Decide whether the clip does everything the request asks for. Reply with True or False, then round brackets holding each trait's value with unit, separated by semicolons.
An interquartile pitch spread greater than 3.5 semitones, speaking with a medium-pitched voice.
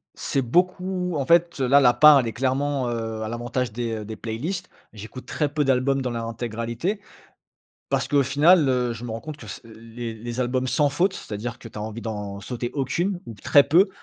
False (4.2 semitones; 125 Hz)